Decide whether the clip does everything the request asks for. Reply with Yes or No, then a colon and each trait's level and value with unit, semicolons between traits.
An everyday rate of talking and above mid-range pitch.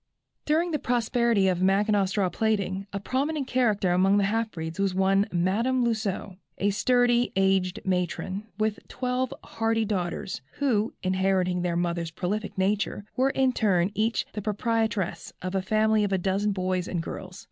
Yes: average, 160 wpm; high, 200 Hz